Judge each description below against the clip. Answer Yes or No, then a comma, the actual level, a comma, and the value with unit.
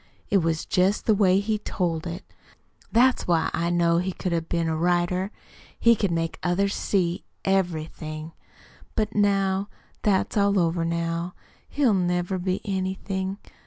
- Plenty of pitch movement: No, average, 2.8 semitones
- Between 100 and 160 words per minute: Yes, average, 150 wpm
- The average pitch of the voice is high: No, medium, 180 Hz